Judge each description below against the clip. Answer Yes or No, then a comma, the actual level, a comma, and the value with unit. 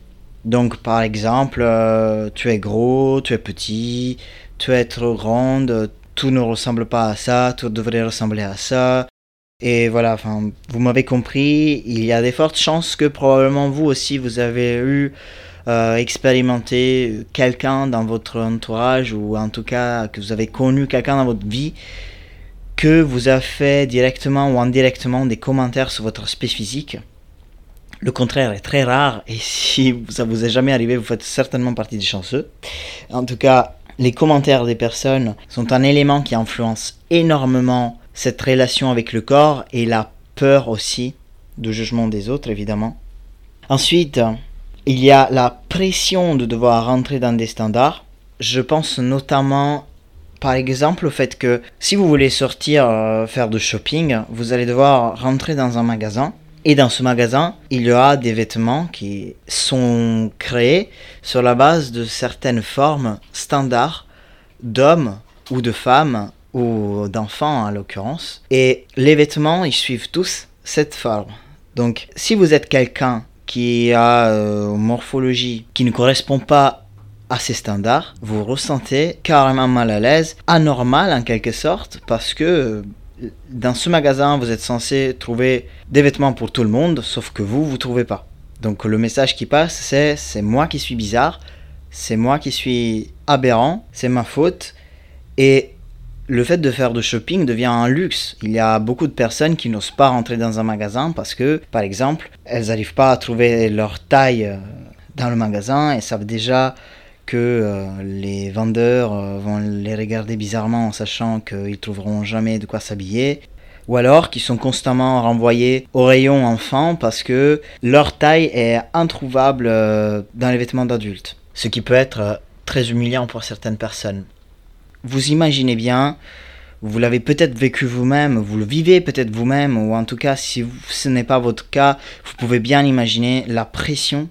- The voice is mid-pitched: No, low, 120 Hz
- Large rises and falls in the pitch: No, average, 3.2 semitones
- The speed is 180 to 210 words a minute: No, average, 165 wpm